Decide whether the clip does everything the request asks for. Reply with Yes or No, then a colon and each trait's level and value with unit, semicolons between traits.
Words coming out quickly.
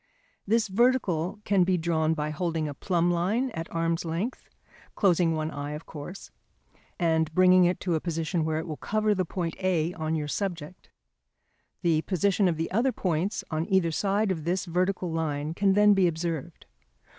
No: average, 180 wpm